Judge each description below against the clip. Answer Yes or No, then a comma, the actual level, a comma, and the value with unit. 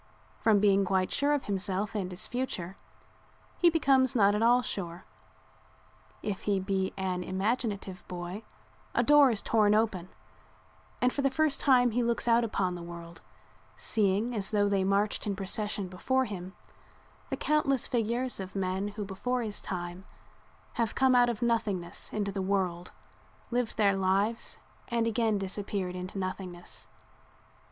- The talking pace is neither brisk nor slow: Yes, average, 155 wpm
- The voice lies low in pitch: No, high, 205 Hz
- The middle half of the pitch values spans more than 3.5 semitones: Yes, average, 3.9 semitones